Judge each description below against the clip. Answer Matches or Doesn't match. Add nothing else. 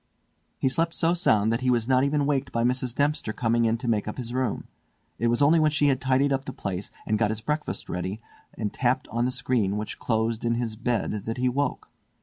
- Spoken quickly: Matches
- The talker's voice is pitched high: Doesn't match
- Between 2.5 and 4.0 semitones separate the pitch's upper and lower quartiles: Matches